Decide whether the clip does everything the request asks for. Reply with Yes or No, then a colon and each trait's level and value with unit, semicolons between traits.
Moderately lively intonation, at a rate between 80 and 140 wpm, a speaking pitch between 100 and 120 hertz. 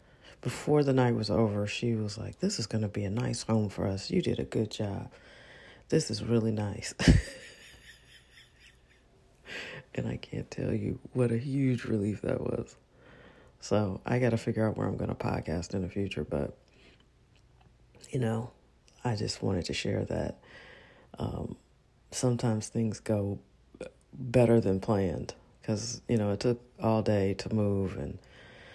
No: average, 3.3 semitones; average, 165 wpm; low, 110 Hz